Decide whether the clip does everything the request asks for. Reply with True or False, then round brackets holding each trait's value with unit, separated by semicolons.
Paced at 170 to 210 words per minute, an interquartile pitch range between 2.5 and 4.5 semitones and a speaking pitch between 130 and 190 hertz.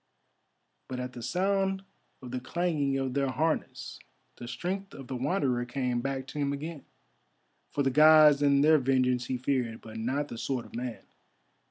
True (175 wpm; 3.2 semitones; 135 Hz)